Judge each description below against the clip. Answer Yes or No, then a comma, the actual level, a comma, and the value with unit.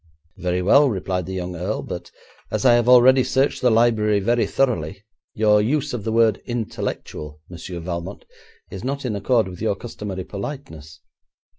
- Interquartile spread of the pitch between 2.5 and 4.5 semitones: No, average, 5.0 semitones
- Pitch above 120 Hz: No, low, 105 Hz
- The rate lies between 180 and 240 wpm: No, average, 165 wpm